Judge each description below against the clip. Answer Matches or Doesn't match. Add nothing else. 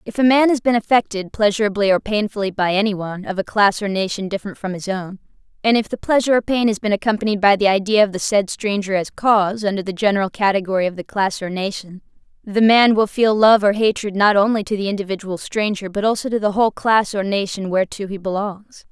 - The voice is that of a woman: Matches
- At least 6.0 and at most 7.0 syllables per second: Matches